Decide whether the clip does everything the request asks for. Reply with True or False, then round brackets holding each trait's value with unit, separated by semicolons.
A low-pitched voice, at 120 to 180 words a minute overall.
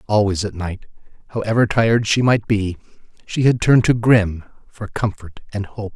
True (105 Hz; 170 wpm)